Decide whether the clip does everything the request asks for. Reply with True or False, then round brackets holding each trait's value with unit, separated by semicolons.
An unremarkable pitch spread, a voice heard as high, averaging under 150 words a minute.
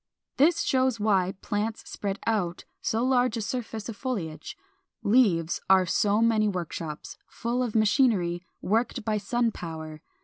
True (4.5 semitones; 215 Hz; 140 wpm)